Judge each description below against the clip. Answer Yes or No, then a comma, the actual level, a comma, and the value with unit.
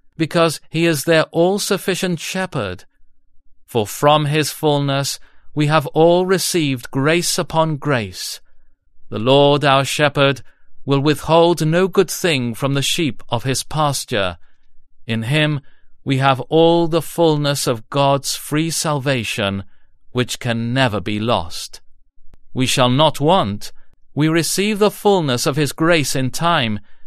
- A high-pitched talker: No, medium, 140 Hz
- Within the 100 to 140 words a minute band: Yes, slow, 135 wpm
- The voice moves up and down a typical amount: No, wide, 6.2 semitones